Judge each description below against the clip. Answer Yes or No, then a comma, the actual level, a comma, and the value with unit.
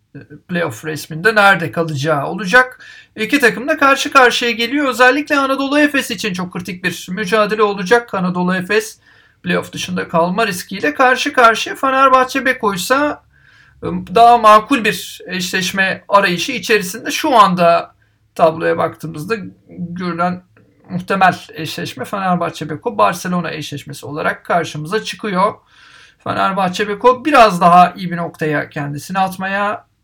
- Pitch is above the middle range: Yes, high, 195 Hz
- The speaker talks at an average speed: Yes, average, 120 wpm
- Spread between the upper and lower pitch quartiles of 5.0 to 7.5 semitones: Yes, wide, 5.5 semitones